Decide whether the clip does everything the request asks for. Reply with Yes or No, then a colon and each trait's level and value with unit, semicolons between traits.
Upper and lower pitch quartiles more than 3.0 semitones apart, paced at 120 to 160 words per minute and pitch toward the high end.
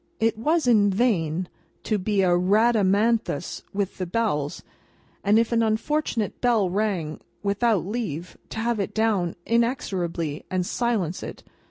Yes: average, 4.0 semitones; average, 140 wpm; high, 205 Hz